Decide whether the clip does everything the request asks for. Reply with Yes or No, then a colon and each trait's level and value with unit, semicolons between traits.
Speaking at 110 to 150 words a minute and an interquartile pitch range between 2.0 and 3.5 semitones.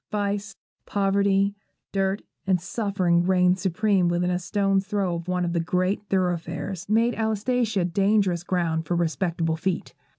Yes: average, 145 wpm; narrow, 2.4 semitones